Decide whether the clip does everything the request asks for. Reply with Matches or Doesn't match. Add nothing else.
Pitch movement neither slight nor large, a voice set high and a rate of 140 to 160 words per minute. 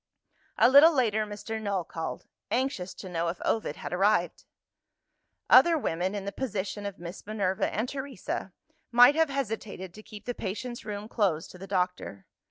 Doesn't match